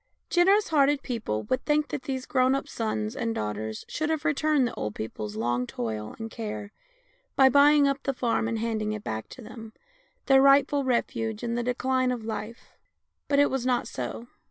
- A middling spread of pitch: Yes, average, 4.3 semitones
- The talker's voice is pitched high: Yes, high, 245 Hz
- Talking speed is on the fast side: No, average, 190 wpm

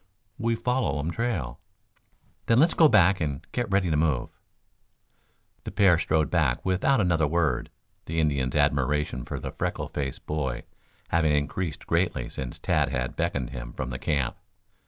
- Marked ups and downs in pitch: Yes, wide, 5.8 semitones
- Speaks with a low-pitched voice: Yes, very low, 75 Hz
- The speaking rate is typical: Yes, average, 155 wpm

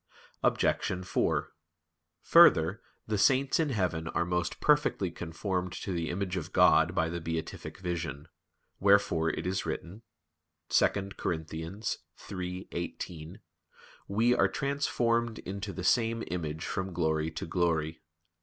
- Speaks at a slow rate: Yes, slow, 125 wpm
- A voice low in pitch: Yes, very low, 90 Hz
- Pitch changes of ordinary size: Yes, average, 3.6 semitones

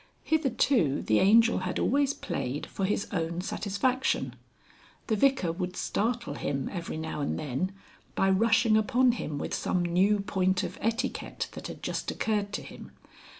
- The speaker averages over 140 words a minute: Yes, average, 155 wpm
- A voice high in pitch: Yes, high, 200 Hz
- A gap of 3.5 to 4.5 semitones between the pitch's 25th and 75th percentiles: No, average, 5.1 semitones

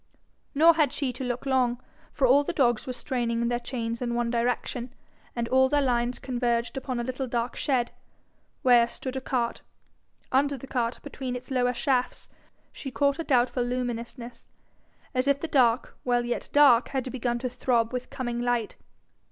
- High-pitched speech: Yes, very high, 250 Hz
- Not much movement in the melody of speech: Yes, narrow, 1.7 semitones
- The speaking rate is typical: Yes, average, 175 wpm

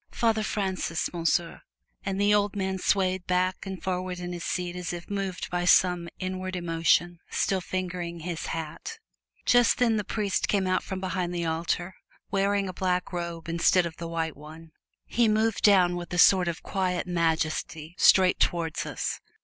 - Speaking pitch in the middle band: Yes, medium, 180 Hz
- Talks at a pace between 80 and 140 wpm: No, average, 175 wpm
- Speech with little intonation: Yes, narrow, 2.0 semitones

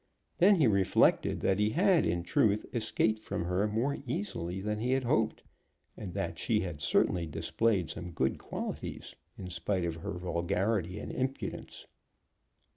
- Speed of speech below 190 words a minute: Yes, average, 155 wpm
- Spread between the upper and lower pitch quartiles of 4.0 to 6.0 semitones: Yes, average, 4.6 semitones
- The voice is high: No, low, 100 Hz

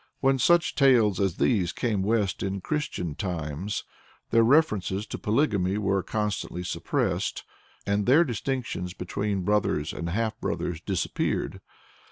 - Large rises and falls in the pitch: No, average, 4.0 semitones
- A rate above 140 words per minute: No, slow, 135 wpm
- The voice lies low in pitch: Yes, low, 105 Hz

